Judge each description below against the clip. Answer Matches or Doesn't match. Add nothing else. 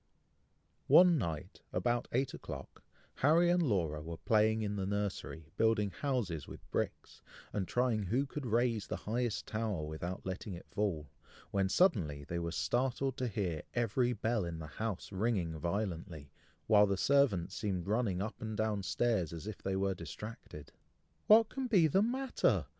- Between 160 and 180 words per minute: Matches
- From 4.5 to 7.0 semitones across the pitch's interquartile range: Matches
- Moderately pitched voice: Doesn't match